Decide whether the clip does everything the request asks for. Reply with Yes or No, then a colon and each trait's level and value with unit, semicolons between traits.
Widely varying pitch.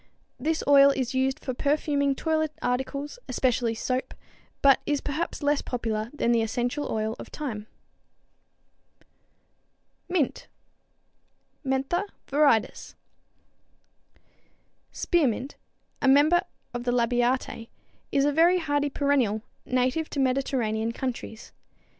No: average, 3.1 semitones